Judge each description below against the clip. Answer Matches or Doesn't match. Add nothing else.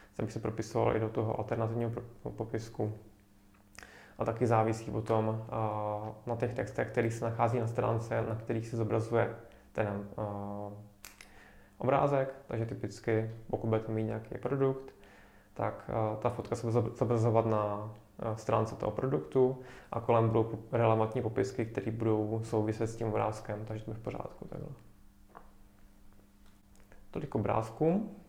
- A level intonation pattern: Matches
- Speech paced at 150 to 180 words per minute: Doesn't match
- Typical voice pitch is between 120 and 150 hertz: Doesn't match